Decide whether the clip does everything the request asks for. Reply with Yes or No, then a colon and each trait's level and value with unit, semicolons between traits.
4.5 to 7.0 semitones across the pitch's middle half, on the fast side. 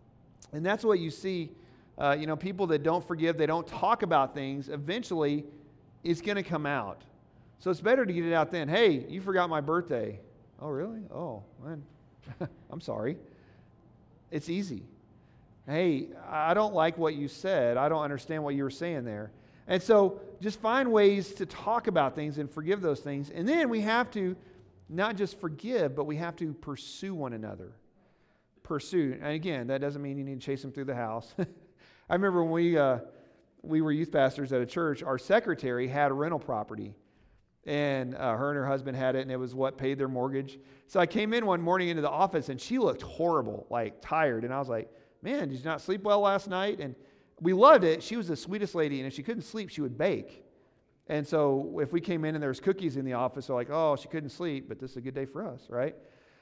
Yes: average, 4.8 semitones; fast, 220 wpm